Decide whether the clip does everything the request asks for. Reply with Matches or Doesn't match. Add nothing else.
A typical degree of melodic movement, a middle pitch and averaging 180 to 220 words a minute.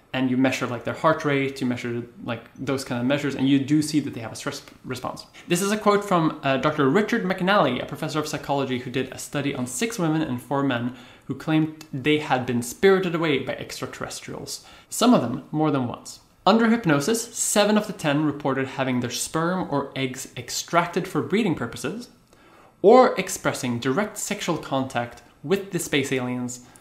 Matches